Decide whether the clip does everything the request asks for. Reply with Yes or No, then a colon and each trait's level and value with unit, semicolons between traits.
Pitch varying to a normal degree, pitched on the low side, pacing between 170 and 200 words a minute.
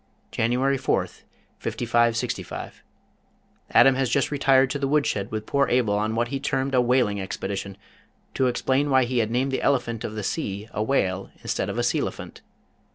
Yes: average, 3.8 semitones; low, 125 Hz; average, 175 wpm